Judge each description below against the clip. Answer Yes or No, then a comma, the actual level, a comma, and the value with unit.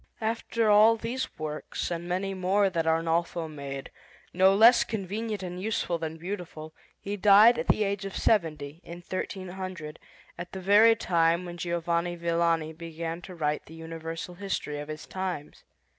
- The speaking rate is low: No, average, 160 wpm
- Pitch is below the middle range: No, medium, 175 Hz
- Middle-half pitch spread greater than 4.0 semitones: No, average, 3.4 semitones